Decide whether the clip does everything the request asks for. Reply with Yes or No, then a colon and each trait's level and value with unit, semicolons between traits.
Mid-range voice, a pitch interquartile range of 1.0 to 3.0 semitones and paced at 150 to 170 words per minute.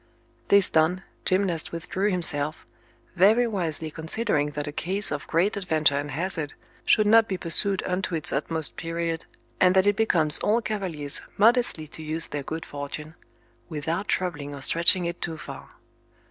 No: medium, 170 Hz; average, 3.9 semitones; average, 160 wpm